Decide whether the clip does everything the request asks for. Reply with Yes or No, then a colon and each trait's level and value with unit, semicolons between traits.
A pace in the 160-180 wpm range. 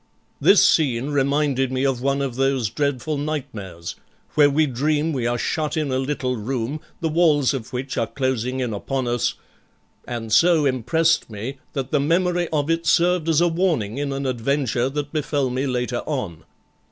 Yes: average, 175 wpm